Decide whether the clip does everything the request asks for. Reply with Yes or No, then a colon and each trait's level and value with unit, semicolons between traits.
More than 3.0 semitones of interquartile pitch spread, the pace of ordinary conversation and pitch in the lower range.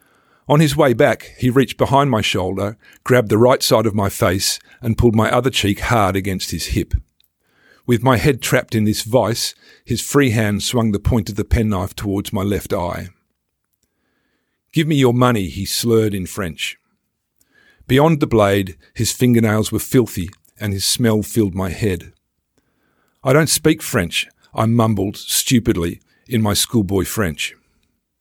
Yes: average, 3.8 semitones; average, 165 wpm; low, 110 Hz